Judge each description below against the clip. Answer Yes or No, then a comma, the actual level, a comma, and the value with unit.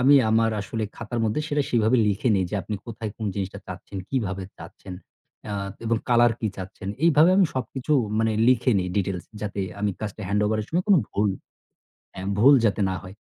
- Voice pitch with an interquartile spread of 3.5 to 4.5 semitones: Yes, average, 3.8 semitones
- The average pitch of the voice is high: No, low, 110 Hz